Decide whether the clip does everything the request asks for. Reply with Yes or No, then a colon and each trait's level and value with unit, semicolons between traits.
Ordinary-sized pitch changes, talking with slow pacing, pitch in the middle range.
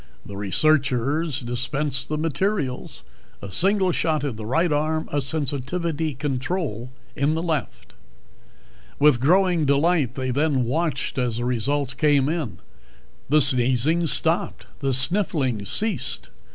Yes: average, 4.2 semitones; slow, 125 wpm; medium, 145 Hz